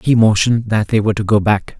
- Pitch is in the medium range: No, low, 110 Hz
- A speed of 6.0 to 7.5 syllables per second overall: Yes, 6.5 syllables/s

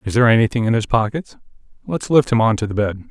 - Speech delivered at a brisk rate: Yes, fast, 230 wpm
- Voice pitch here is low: Yes, low, 115 Hz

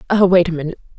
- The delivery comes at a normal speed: No, fast, 245 wpm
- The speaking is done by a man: No, female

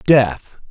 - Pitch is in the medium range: No, low, 110 Hz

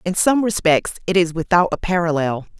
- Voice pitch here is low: No, medium, 175 Hz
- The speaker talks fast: No, average, 185 wpm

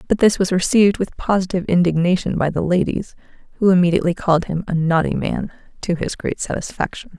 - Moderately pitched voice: Yes, medium, 180 Hz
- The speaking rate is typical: Yes, average, 175 wpm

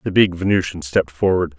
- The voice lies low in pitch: Yes, very low, 85 Hz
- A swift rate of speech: No, average, 190 wpm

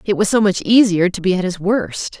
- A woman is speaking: Yes, female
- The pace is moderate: No, fast, 275 wpm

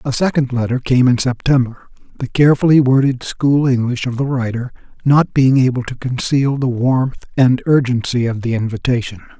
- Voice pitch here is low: Yes, low, 125 Hz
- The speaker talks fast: No, average, 165 wpm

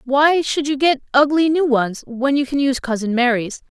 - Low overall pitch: No, very high, 270 Hz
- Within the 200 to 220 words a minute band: Yes, fast, 205 wpm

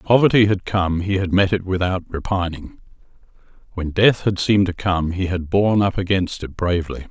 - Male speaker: Yes, male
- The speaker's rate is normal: Yes, average, 195 wpm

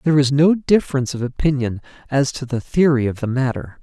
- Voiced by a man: Yes, male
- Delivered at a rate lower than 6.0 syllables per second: No, 6.1 syllables/s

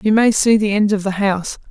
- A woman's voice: Yes, female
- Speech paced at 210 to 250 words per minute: No, fast, 280 wpm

